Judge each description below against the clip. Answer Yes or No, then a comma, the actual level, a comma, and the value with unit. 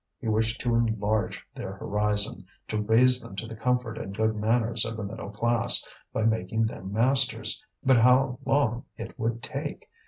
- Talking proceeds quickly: No, average, 175 wpm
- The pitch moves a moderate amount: No, narrow, 2.3 semitones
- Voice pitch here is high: No, low, 115 Hz